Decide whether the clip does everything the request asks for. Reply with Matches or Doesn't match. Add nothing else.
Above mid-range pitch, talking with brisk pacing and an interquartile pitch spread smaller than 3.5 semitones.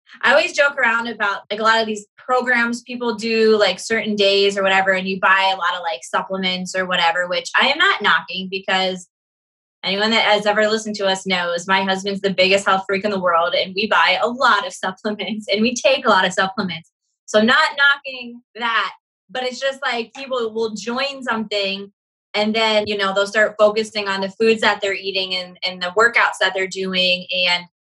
Matches